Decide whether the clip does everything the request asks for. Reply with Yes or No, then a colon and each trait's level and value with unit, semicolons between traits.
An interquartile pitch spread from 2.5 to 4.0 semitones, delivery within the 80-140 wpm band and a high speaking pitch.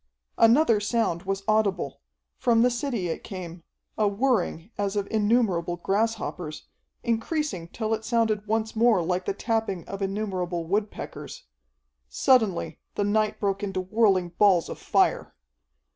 Yes: average, 3.3 semitones; slow, 135 wpm; high, 205 Hz